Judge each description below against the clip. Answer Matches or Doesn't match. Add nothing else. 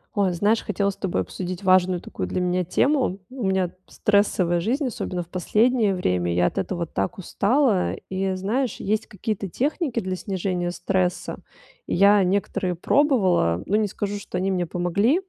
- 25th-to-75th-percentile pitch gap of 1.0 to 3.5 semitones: Matches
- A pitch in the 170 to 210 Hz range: Matches